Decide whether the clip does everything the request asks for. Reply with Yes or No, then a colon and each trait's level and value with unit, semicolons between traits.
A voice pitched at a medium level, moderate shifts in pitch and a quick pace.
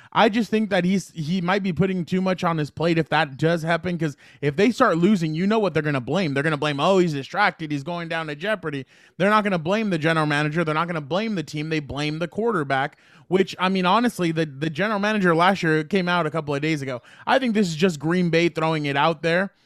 Yes: medium, 170 Hz; average, 3.3 semitones; fast, 270 wpm